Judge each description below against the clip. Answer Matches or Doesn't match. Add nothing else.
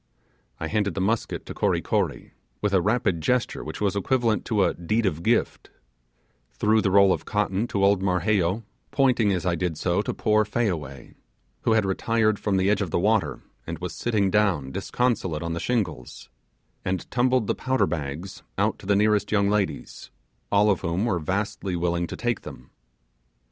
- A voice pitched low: Matches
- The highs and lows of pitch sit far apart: Doesn't match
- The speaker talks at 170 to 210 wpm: Matches